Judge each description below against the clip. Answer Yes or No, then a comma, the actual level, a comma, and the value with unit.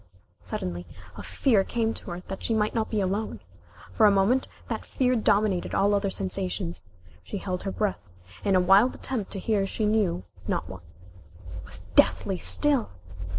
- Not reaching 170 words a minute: No, average, 175 wpm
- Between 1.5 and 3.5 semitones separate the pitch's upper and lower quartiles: Yes, average, 3.1 semitones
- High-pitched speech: Yes, high, 195 Hz